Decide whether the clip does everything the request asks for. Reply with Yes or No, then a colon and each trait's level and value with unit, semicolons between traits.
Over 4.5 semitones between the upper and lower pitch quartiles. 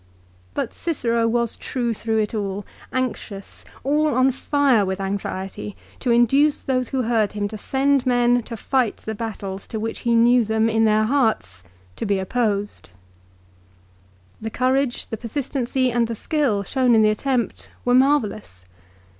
No: average, 3.4 semitones